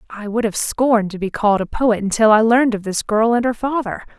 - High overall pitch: Yes, high, 220 Hz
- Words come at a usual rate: No, fast, 260 wpm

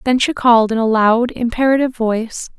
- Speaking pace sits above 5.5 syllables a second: Yes, 5.8 syllables/s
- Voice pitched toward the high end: Yes, high, 235 Hz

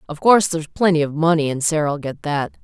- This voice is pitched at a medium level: Yes, medium, 160 Hz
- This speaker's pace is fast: Yes, fast, 225 wpm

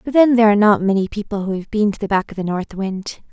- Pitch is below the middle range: No, high, 205 Hz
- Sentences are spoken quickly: Yes, fast, 305 wpm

